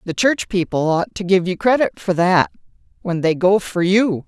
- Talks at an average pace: No, fast, 210 wpm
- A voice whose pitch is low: No, medium, 185 Hz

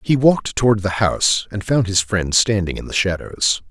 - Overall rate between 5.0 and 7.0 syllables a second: Yes, 5.1 syllables/s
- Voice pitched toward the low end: Yes, low, 105 Hz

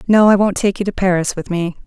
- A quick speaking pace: Yes, fast, 290 wpm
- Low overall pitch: No, high, 190 Hz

